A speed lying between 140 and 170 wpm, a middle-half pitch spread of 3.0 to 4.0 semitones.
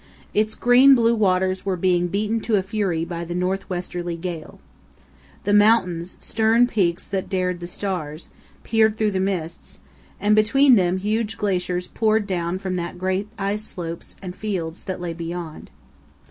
Yes: average, 160 wpm; average, 3.3 semitones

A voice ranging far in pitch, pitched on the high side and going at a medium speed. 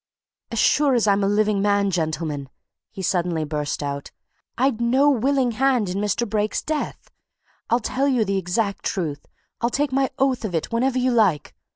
Yes: wide, 6.0 semitones; high, 215 Hz; average, 180 wpm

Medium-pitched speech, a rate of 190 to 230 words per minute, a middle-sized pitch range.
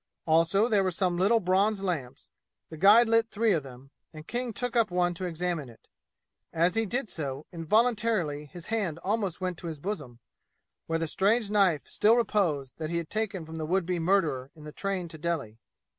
Yes: medium, 180 Hz; average, 200 wpm; average, 4.8 semitones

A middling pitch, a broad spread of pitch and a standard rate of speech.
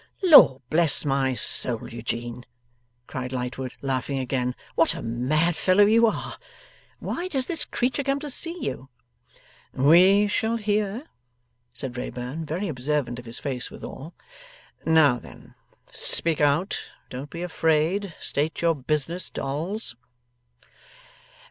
No: medium, 155 Hz; wide, 7.4 semitones; slow, 125 wpm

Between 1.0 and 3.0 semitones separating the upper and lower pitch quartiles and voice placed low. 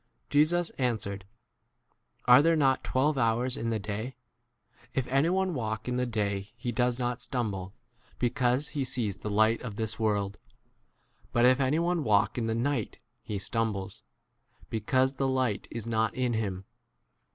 No: average, 3.5 semitones; low, 120 Hz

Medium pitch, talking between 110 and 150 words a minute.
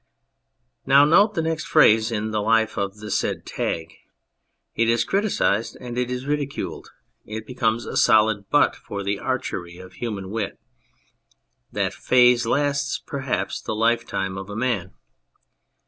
No: low, 115 Hz; average, 145 wpm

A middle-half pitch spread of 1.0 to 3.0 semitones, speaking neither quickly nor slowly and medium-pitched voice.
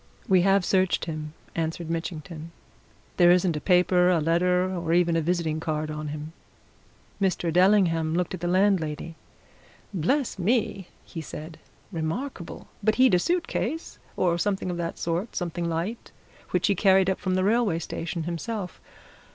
Yes: average, 2.7 semitones; average, 160 wpm; medium, 175 Hz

